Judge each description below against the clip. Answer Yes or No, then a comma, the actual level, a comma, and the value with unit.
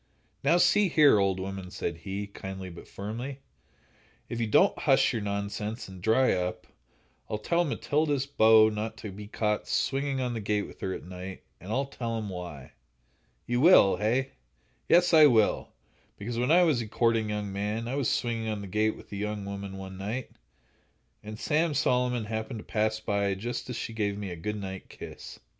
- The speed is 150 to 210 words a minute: Yes, average, 190 wpm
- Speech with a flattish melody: No, average, 3.8 semitones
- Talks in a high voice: No, low, 110 Hz